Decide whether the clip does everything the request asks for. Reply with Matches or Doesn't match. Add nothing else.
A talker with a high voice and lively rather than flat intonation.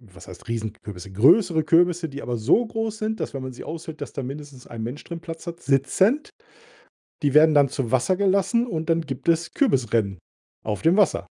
Doesn't match